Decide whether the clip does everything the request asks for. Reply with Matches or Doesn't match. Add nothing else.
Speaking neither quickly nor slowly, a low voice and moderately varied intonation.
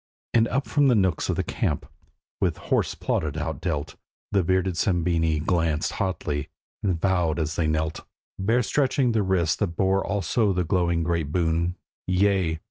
Matches